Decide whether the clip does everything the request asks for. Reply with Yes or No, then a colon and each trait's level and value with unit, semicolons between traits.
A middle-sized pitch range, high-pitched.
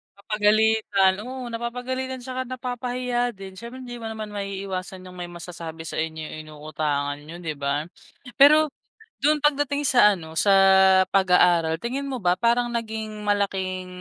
No: wide, 5.7 semitones; high, 210 Hz